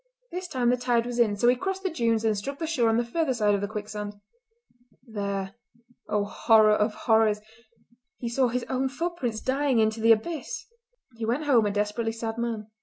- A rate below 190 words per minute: No, average, 200 wpm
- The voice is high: Yes, high, 230 Hz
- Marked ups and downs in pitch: No, average, 3.2 semitones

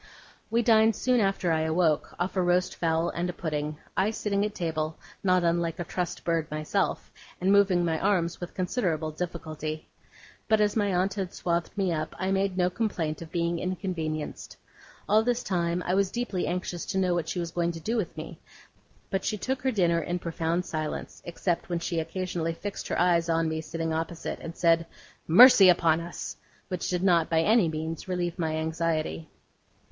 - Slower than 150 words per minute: No, average, 190 wpm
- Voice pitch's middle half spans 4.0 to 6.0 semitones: No, average, 2.7 semitones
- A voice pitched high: No, medium, 175 Hz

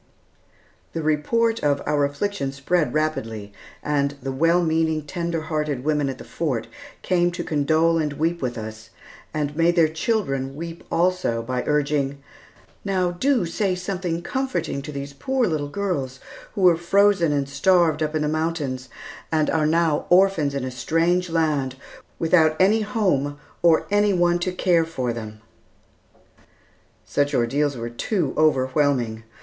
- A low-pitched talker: No, medium, 155 Hz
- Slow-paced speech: No, average, 150 wpm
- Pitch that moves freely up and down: No, average, 3.9 semitones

